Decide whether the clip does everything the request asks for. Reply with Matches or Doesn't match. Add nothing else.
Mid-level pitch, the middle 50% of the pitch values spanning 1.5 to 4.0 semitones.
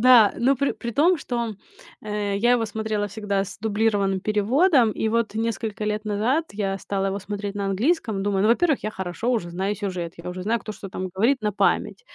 Doesn't match